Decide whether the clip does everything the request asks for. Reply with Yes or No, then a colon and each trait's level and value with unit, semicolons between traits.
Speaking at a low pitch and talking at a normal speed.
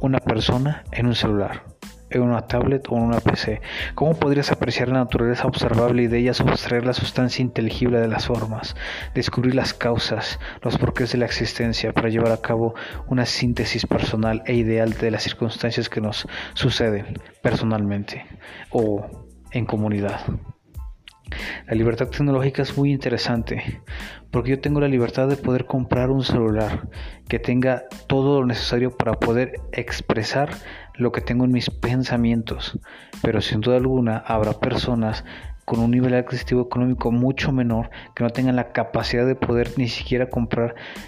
Yes: low, 120 Hz; average, 160 wpm